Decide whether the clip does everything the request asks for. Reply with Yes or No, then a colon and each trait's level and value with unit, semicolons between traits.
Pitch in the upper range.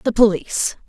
Yes: high, 215 Hz